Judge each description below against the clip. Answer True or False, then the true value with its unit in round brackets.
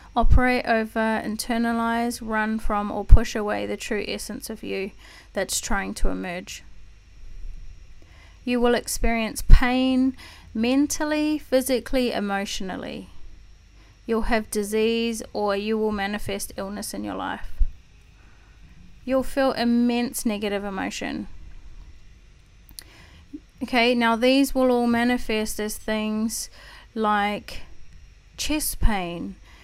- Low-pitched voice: False (215 Hz)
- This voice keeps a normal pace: False (105 wpm)